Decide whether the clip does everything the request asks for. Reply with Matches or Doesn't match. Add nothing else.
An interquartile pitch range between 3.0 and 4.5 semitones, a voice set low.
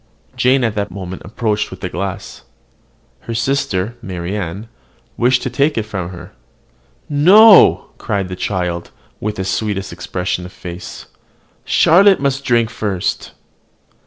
Doesn't match